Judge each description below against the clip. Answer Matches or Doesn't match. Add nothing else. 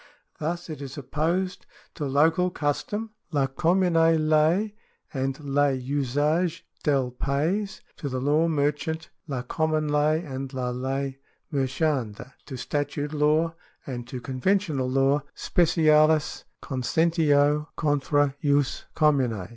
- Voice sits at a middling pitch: Matches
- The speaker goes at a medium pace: Doesn't match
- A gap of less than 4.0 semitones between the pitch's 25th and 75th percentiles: Matches